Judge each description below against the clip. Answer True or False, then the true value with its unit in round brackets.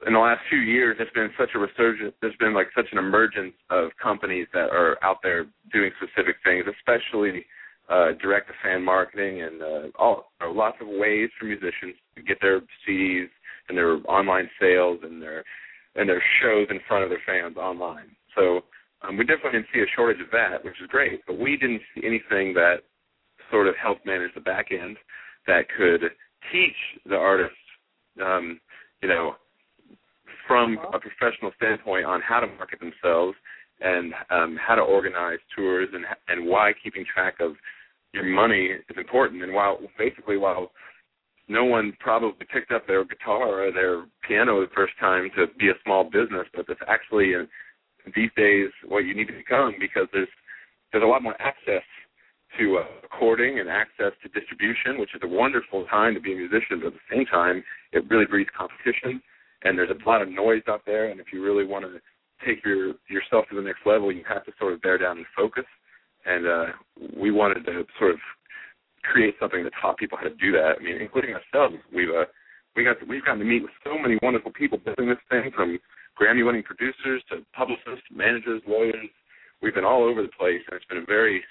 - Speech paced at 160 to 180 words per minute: False (195 wpm)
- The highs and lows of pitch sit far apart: False (4.0 semitones)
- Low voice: True (100 Hz)